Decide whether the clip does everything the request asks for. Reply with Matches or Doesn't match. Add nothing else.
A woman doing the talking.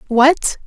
Matches